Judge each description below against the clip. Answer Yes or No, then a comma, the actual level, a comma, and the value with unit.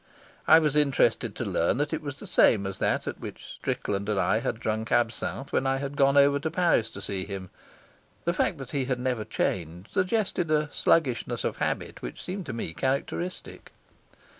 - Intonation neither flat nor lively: No, wide, 5.8 semitones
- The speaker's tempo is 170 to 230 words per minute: Yes, average, 195 wpm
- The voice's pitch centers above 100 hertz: Yes, low, 135 Hz